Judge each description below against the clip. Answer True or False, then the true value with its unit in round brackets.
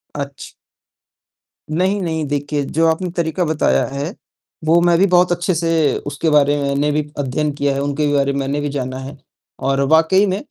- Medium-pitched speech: True (150 Hz)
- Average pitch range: True (3.0 semitones)